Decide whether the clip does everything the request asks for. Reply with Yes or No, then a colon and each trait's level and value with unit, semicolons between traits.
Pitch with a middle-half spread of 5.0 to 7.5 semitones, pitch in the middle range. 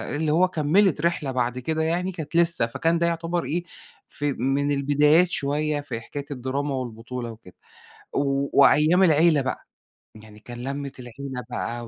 No: average, 4.2 semitones; medium, 145 Hz